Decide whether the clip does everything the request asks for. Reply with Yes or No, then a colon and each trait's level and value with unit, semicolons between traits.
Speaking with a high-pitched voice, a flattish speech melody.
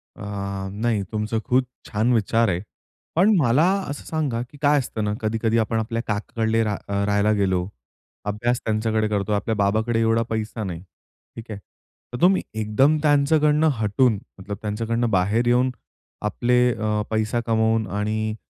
No: low, 110 Hz; narrow, 2.3 semitones